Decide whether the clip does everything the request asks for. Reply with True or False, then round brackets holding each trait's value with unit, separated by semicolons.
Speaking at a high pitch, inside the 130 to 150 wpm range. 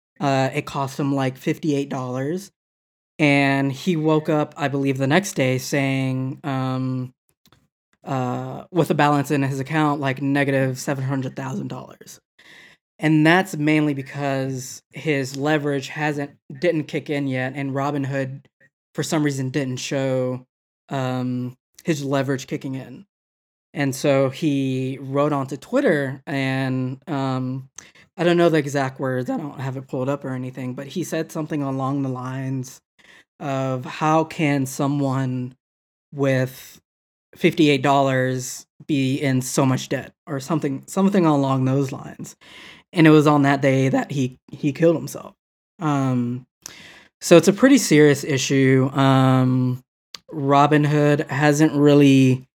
False (140 Hz; 145 wpm)